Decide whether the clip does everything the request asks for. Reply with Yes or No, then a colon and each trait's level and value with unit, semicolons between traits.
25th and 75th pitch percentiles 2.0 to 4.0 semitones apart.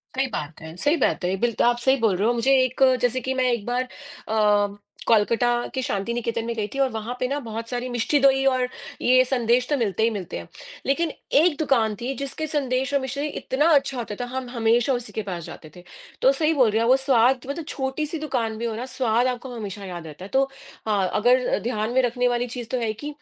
Yes: average, 3.1 semitones